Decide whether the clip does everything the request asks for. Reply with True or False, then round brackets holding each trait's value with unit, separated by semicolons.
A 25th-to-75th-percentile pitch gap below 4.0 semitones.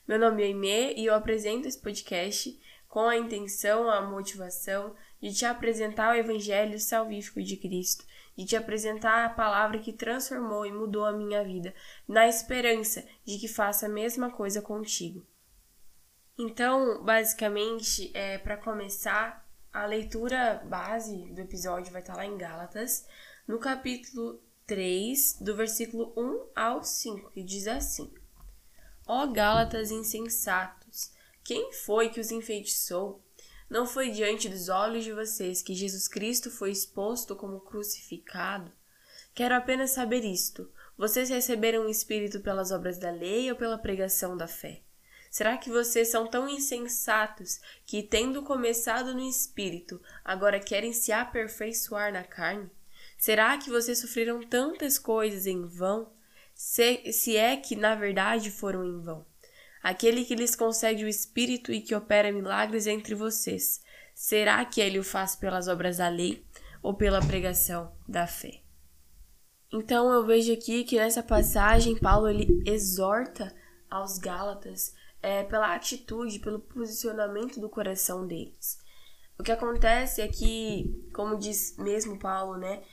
True (2.7 semitones)